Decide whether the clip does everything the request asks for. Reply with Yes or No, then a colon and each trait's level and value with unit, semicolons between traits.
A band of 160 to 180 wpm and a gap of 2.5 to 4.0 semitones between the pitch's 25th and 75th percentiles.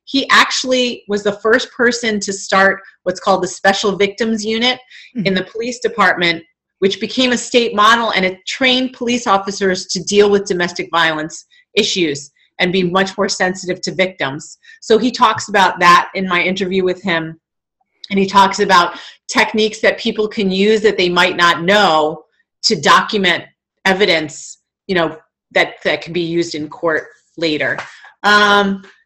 Yes: average, 165 wpm; average, 3.6 semitones